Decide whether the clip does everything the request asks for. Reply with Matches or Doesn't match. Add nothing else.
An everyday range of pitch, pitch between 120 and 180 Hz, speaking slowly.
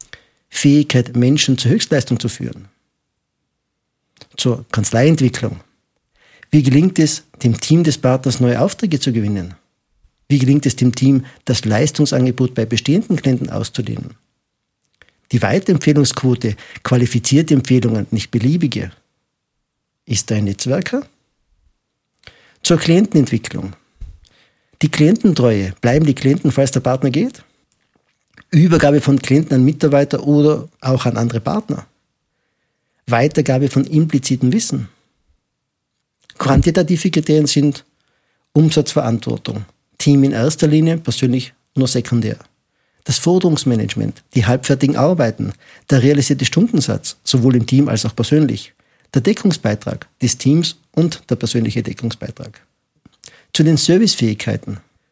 Matches